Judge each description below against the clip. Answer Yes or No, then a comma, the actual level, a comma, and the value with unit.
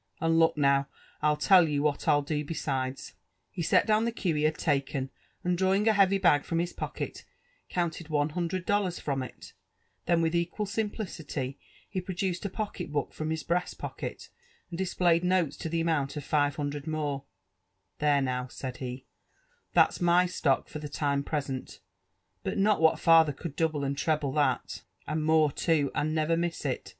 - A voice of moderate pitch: Yes, medium, 160 Hz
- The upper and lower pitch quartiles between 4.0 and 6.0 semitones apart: No, average, 3.3 semitones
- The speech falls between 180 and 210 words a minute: Yes, average, 195 wpm